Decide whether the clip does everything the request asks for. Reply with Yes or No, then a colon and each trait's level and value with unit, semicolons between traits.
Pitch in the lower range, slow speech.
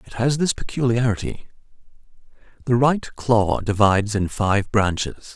Yes: low, 115 Hz; slow, 110 wpm